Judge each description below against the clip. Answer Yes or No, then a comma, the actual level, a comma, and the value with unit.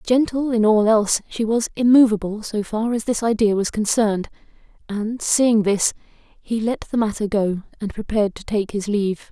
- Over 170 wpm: Yes, average, 180 wpm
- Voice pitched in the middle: No, high, 215 Hz